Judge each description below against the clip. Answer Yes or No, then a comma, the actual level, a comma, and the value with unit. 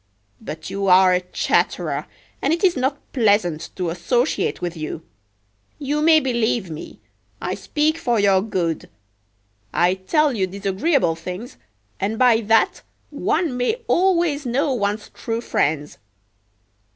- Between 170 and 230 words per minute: No, slow, 135 wpm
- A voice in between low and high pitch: No, high, 220 Hz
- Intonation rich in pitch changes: Yes, wide, 7.4 semitones